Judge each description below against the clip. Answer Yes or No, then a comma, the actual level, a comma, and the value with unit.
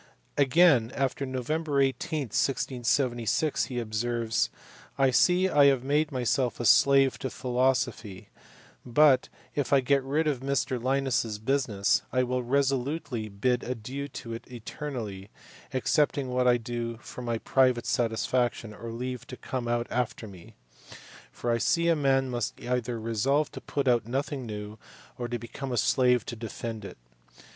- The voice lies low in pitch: Yes, low, 125 Hz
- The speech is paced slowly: No, average, 155 wpm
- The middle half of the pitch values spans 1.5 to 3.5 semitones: Yes, average, 2.8 semitones